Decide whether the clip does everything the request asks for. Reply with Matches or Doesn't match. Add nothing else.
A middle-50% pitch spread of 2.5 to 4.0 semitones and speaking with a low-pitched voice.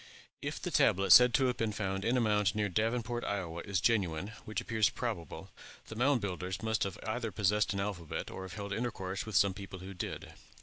Matches